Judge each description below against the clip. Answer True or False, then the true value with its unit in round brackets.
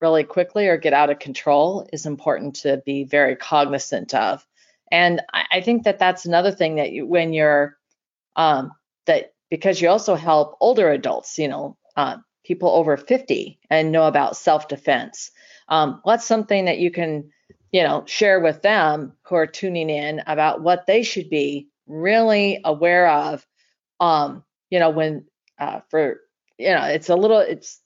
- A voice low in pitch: False (160 Hz)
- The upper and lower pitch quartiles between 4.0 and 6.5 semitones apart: False (3.6 semitones)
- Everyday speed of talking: True (170 wpm)